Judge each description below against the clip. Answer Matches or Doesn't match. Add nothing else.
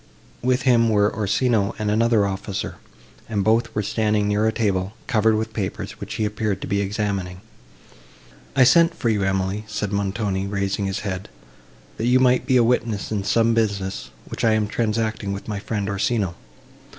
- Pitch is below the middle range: Matches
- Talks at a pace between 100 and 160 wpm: Doesn't match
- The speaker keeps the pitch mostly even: Matches